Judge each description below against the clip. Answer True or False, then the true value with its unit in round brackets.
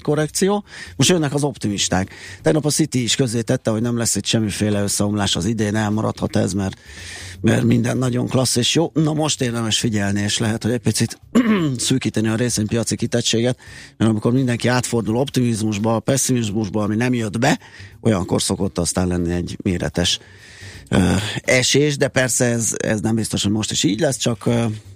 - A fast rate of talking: True (175 wpm)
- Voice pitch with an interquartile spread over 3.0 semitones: True (3.6 semitones)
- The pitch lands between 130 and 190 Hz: False (115 Hz)